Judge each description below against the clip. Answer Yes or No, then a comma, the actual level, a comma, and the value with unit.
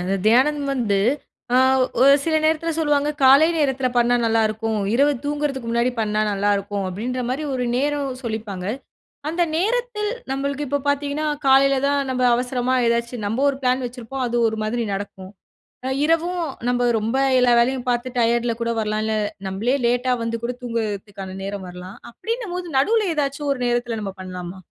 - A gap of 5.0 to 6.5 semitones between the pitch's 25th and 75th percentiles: No, average, 4.3 semitones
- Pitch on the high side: Yes, very high, 250 Hz